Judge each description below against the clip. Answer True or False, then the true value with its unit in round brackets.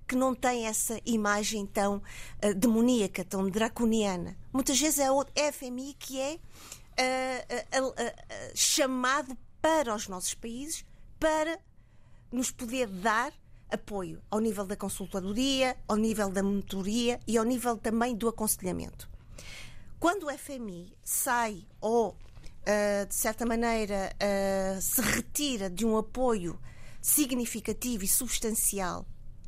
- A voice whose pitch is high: True (225 Hz)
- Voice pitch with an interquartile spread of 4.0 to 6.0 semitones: True (4.3 semitones)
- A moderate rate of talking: True (130 wpm)